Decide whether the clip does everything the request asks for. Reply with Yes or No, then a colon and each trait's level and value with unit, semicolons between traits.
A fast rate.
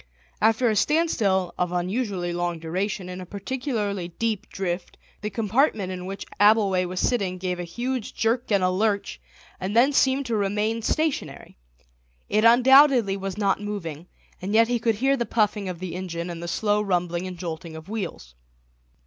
No: average, 175 wpm